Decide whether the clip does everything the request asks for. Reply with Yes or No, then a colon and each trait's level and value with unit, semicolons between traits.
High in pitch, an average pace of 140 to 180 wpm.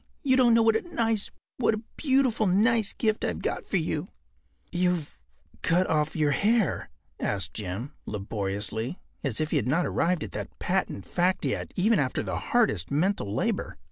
No: medium, 175 Hz; average, 170 wpm